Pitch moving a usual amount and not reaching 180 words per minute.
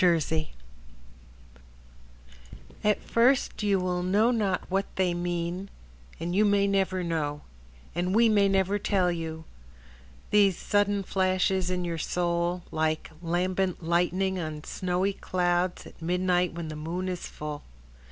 No: narrow, 2.1 semitones; slow, 135 wpm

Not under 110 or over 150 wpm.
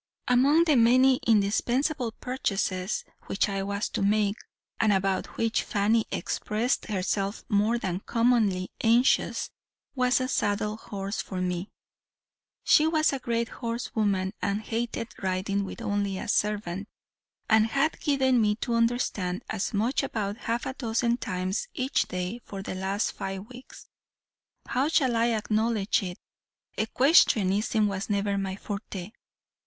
Yes: average, 140 wpm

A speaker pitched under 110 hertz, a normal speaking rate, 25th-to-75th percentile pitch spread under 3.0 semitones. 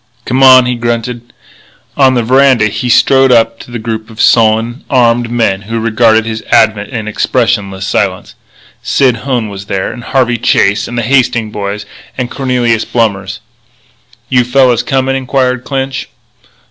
No: low, 120 Hz; average, 155 wpm; narrow, 2.6 semitones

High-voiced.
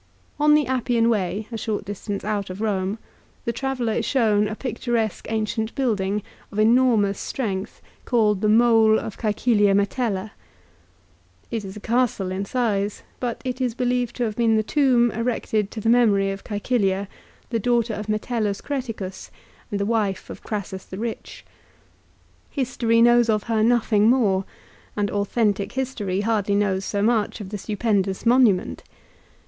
Yes: high, 220 Hz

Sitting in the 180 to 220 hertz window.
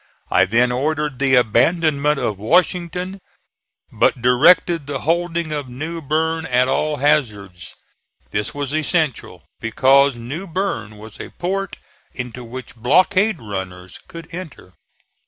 No: medium, 140 Hz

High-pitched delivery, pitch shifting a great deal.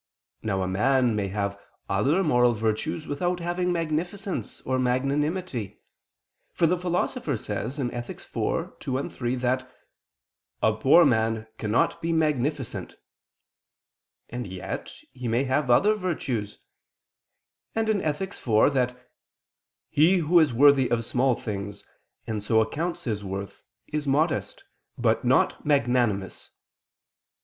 No: low, 130 Hz; wide, 5.9 semitones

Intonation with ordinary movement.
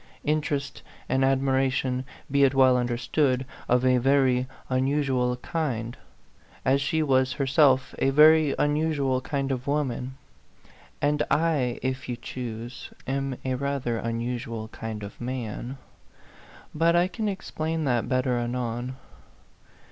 No: narrow, 2.3 semitones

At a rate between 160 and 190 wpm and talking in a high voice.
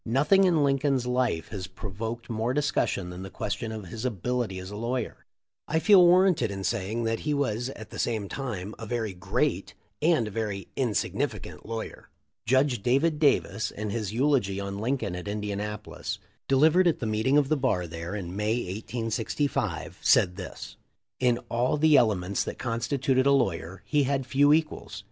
No: average, 175 wpm; low, 115 Hz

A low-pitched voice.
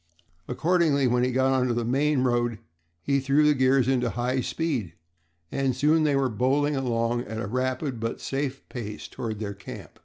Yes: low, 130 Hz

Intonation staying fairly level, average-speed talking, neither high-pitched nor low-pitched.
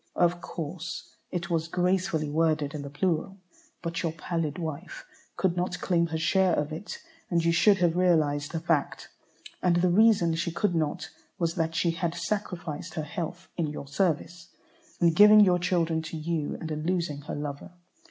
Yes: narrow, 2.2 semitones; average, 180 wpm; medium, 170 Hz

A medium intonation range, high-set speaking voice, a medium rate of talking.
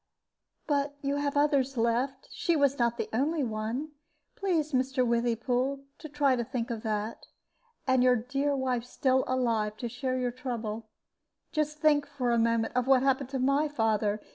Yes: average, 3.2 semitones; very high, 255 Hz; average, 170 wpm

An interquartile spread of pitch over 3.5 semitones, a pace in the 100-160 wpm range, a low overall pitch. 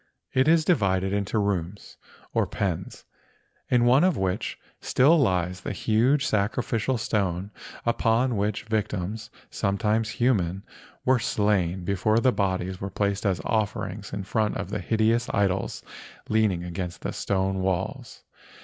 No: average, 3.1 semitones; slow, 135 wpm; low, 105 Hz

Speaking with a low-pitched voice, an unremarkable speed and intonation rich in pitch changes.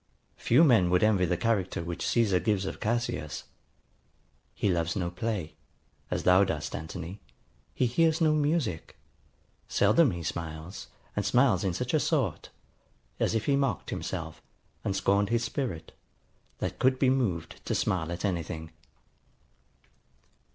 Yes: low, 100 Hz; average, 150 wpm; wide, 6.2 semitones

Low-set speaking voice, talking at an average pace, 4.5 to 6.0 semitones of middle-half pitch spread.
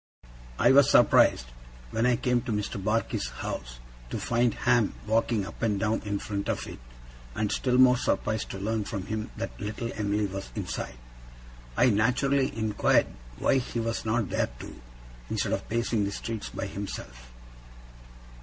No: low, 110 Hz; average, 165 wpm; average, 2.7 semitones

